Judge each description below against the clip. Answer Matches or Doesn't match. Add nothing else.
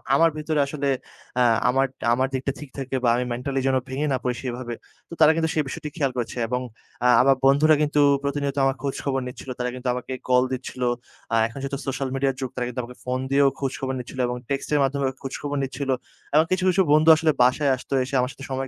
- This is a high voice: Doesn't match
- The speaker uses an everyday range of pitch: Doesn't match